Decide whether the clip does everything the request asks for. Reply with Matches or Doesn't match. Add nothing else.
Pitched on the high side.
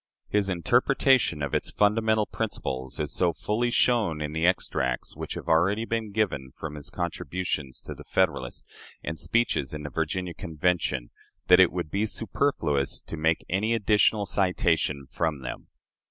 Doesn't match